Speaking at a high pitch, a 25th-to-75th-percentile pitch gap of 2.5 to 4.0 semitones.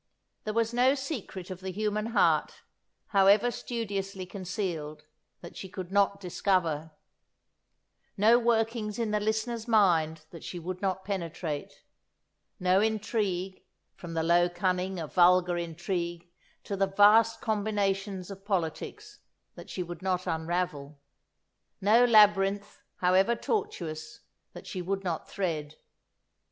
Yes: high, 195 Hz; average, 3.4 semitones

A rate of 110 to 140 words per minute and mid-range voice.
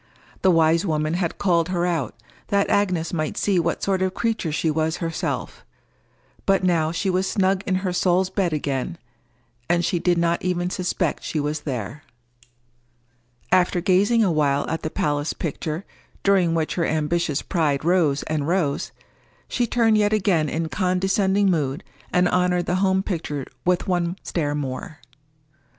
No: average, 160 wpm; medium, 175 Hz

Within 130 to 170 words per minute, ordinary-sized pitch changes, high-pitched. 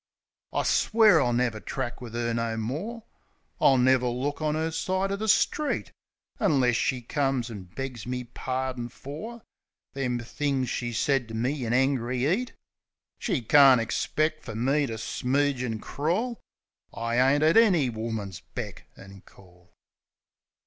No: average, 155 wpm; average, 4.3 semitones; low, 130 Hz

